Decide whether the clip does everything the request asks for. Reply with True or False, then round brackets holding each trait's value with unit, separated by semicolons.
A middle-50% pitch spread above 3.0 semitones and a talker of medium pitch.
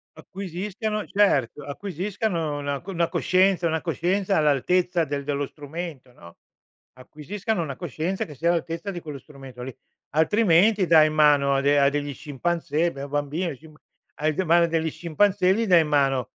True (4.1 semitones; 160 Hz)